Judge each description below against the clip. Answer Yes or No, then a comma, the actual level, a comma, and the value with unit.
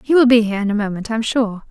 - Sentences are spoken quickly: Yes, fast, 350 wpm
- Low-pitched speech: No, high, 225 Hz